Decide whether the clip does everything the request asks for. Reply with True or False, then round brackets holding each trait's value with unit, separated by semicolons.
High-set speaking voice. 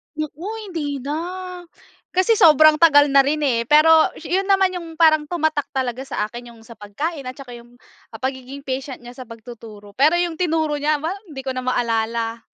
True (285 Hz)